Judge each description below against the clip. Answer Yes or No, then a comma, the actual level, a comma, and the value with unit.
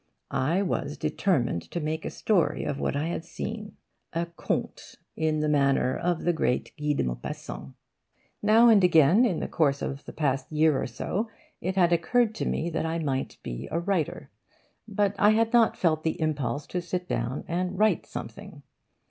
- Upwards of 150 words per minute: Yes, average, 180 wpm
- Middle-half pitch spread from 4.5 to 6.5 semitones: Yes, average, 4.8 semitones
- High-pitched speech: No, medium, 165 Hz